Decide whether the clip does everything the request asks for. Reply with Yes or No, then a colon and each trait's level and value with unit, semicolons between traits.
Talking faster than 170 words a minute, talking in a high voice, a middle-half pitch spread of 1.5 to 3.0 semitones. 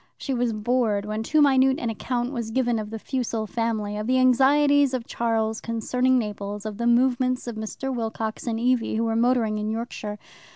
Yes: average, 195 wpm; high, 235 Hz; average, 2.7 semitones